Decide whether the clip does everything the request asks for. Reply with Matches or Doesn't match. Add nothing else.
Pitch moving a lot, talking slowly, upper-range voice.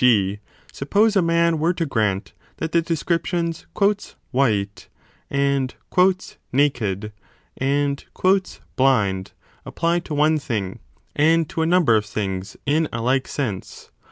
Doesn't match